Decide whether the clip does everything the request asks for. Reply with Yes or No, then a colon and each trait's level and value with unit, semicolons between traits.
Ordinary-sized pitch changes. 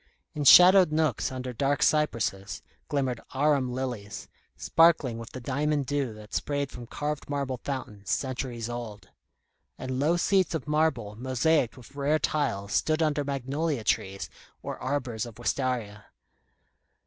Yes: average, 4.0 semitones